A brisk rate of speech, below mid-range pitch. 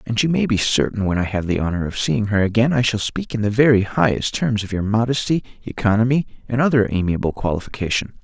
Yes: fast, 220 wpm; low, 110 Hz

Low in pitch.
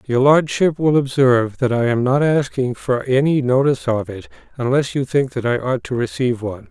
Yes: low, 130 Hz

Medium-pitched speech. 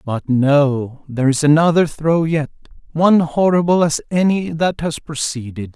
Yes: medium, 150 Hz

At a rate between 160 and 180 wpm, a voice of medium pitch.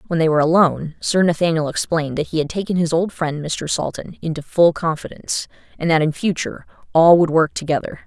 No: average, 200 wpm; medium, 165 Hz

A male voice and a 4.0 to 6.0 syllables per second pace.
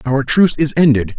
Yes: male; 5.8 syllables/s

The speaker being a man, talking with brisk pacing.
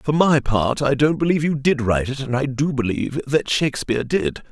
Yes: male; fast, 225 wpm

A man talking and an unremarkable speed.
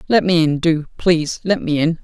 No: male; fast, 235 wpm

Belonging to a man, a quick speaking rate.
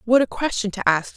No: female; fast, 260 wpm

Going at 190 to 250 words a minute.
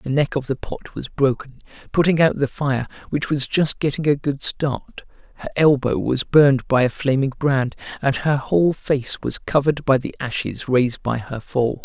Yes: average, 200 wpm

